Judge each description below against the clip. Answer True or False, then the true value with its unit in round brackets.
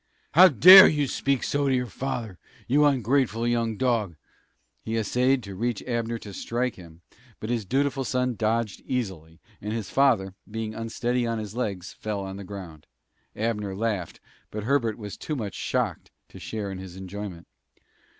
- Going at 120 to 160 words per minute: False (170 wpm)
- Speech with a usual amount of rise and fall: True (4.1 semitones)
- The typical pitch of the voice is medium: False (115 Hz)